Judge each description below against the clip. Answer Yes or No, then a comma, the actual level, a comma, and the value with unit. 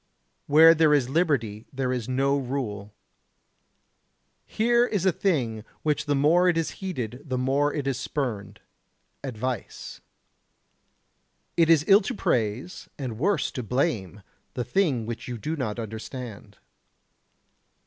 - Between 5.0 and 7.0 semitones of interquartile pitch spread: Yes, average, 5.3 semitones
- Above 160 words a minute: No, slow, 135 wpm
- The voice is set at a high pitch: No, low, 135 Hz